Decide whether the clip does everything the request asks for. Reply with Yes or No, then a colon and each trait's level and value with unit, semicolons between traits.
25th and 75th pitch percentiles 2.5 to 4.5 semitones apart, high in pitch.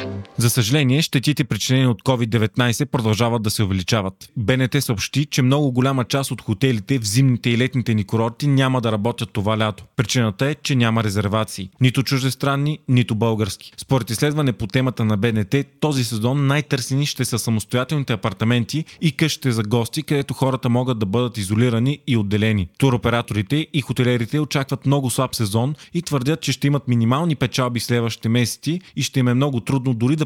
No: average, 3.3 semitones; low, 125 Hz